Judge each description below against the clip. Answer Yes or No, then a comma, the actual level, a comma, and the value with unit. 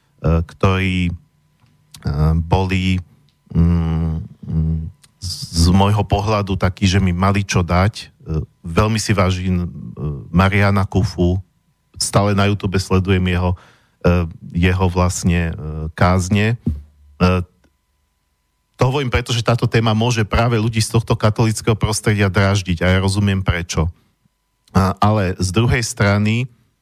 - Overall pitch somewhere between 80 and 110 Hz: Yes, very low, 95 Hz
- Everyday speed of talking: No, slow, 105 wpm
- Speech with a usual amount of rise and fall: Yes, average, 3.4 semitones